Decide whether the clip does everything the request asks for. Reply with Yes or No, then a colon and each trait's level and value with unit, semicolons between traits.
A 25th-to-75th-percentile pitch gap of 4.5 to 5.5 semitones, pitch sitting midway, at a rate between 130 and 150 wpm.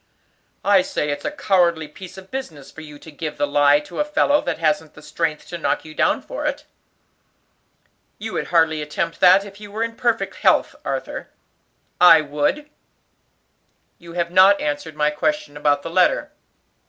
No: average, 5.2 semitones; medium, 165 Hz; average, 180 wpm